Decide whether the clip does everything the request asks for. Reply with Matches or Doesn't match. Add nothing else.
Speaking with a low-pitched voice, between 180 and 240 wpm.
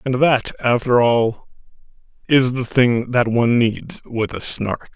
Doesn't match